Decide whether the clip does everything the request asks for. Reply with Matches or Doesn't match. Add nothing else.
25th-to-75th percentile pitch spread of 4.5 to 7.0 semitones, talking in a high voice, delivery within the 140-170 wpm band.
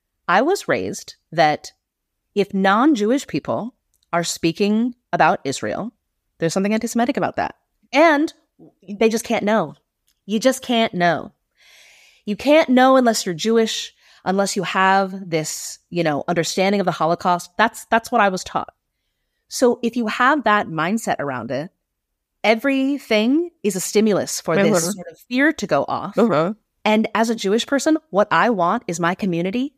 Matches